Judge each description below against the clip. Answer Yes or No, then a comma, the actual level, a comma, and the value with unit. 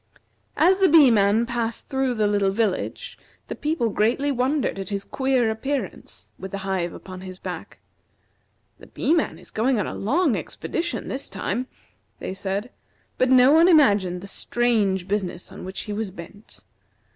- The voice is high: Yes, high, 220 Hz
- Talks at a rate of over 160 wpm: Yes, average, 170 wpm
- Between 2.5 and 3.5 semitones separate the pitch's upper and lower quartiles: No, wide, 5.4 semitones